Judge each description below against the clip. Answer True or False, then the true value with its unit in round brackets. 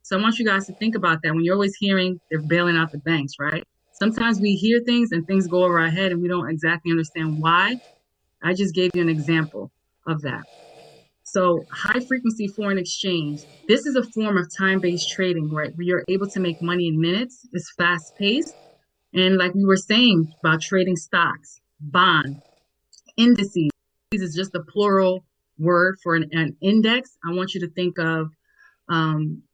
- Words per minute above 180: True (190 wpm)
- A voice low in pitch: False (180 Hz)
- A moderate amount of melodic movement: True (3.5 semitones)